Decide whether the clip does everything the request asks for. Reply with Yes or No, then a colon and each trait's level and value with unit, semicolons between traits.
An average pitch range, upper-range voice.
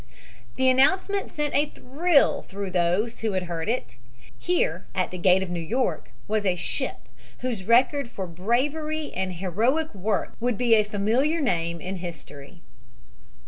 No: wide, 6.5 semitones; high, 210 Hz